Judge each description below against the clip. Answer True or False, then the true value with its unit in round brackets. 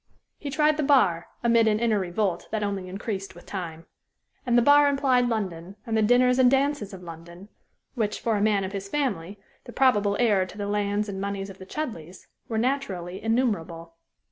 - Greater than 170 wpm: True (195 wpm)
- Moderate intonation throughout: True (4.5 semitones)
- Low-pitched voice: False (210 Hz)